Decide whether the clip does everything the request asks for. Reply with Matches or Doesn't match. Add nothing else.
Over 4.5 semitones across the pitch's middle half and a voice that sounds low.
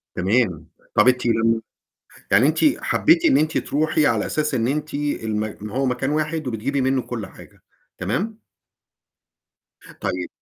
Matches